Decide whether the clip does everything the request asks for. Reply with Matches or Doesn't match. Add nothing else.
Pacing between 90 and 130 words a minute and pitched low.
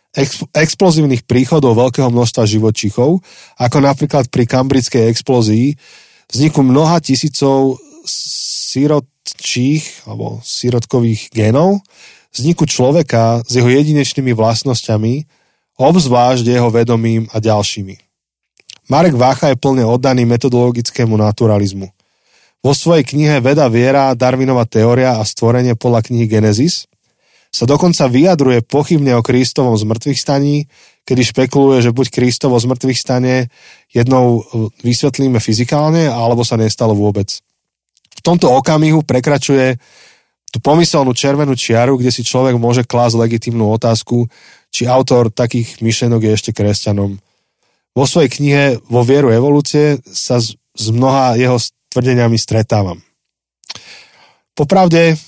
Matches